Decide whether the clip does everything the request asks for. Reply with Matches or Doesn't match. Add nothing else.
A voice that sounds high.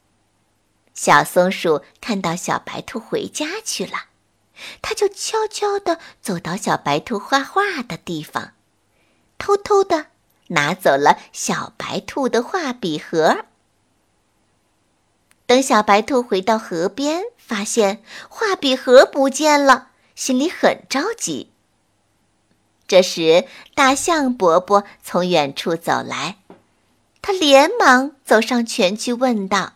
Matches